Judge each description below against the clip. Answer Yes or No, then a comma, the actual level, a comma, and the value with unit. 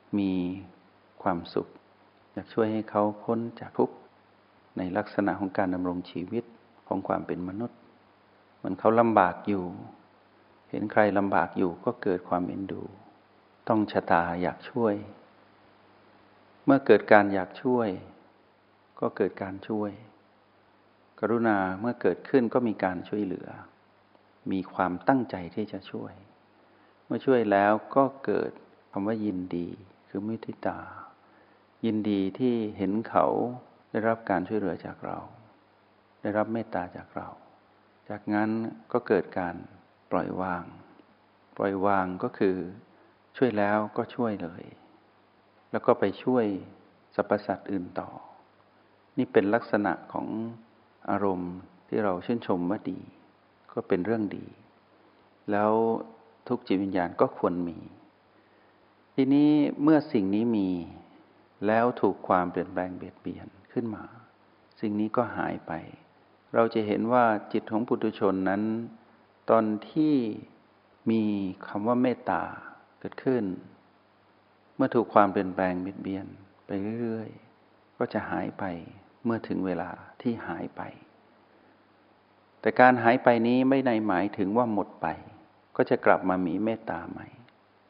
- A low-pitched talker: Yes, low, 105 Hz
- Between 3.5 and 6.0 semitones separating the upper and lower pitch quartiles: No, average, 3.0 semitones